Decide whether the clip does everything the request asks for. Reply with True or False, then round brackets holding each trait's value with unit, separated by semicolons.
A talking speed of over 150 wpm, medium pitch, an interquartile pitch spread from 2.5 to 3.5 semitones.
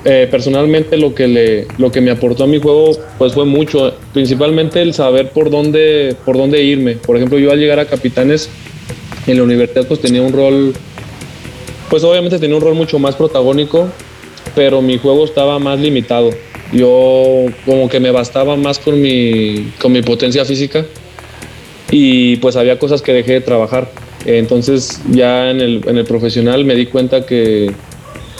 False (175 wpm; 130 Hz; 2.8 semitones)